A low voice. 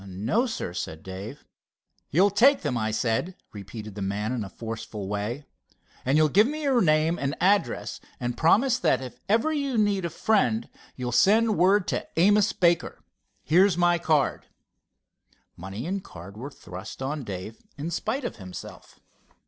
No: medium, 155 Hz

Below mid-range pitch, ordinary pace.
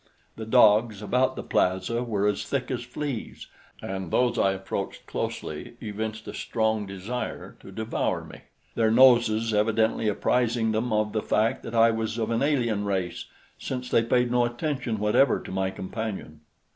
Yes: low, 110 Hz; average, 165 wpm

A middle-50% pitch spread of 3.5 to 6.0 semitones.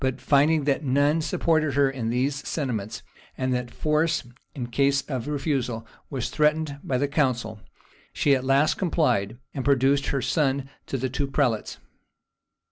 No: narrow, 2.6 semitones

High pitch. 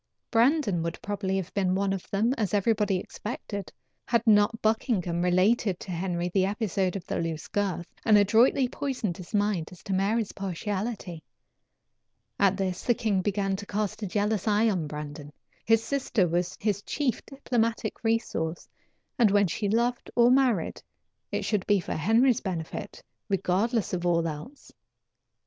Yes: high, 200 Hz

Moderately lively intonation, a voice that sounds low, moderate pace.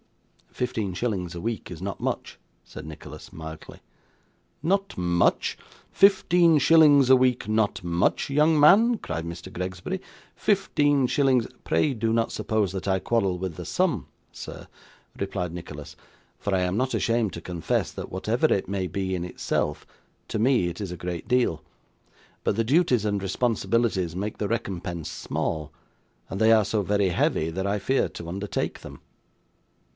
No: wide, 5.8 semitones; low, 100 Hz; average, 165 wpm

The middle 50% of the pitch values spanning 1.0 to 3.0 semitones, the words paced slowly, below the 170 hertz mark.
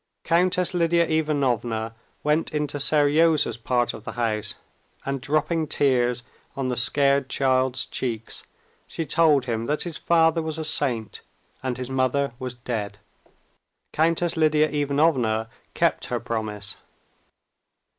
No: average, 4.4 semitones; slow, 125 wpm; medium, 140 Hz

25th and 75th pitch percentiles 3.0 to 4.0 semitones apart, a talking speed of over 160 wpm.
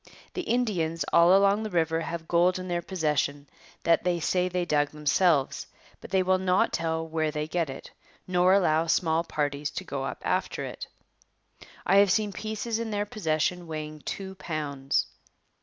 Yes: average, 3.4 semitones; average, 175 wpm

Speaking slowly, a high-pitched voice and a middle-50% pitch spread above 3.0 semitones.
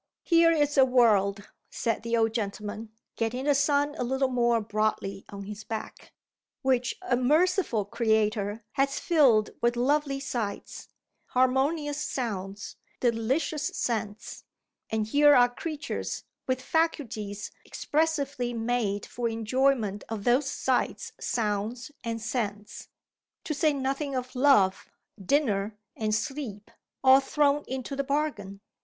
Yes: slow, 125 wpm; high, 245 Hz; average, 4.5 semitones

